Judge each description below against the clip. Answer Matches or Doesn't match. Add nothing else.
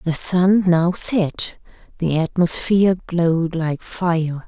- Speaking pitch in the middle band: Matches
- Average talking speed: Doesn't match